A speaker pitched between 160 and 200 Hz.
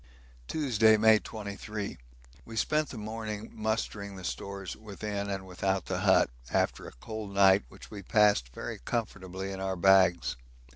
No: low, 100 Hz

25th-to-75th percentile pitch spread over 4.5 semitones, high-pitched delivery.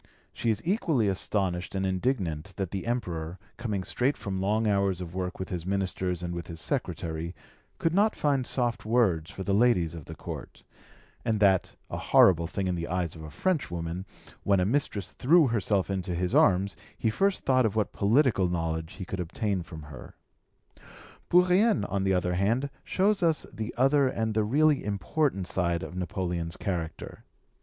No: average, 5.3 semitones; very low, 95 Hz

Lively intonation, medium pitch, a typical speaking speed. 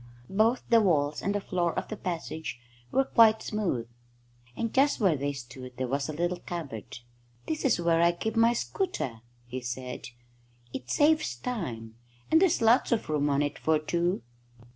Yes: wide, 8.8 semitones; medium, 170 Hz; average, 175 wpm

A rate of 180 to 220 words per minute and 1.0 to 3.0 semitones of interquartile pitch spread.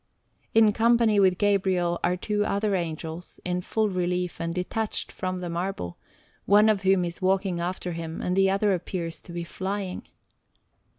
No: average, 165 wpm; narrow, 2.6 semitones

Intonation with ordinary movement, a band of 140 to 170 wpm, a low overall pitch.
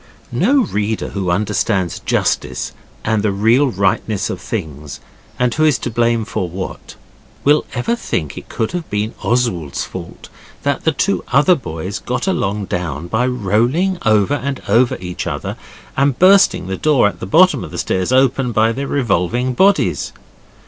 No: wide, 6.1 semitones; average, 165 wpm; low, 115 Hz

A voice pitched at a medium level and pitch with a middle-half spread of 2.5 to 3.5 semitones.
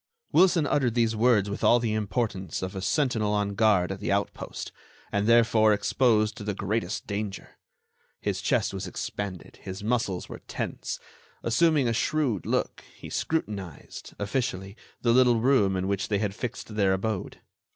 No: low, 105 Hz; average, 3.2 semitones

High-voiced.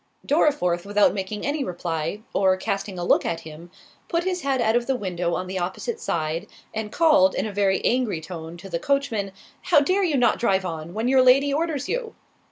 Yes: high, 210 Hz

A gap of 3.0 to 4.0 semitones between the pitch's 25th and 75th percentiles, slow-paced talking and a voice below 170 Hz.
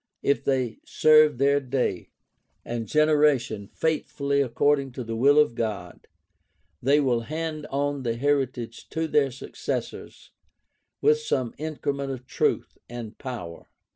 Yes: average, 3.7 semitones; slow, 130 wpm; low, 135 Hz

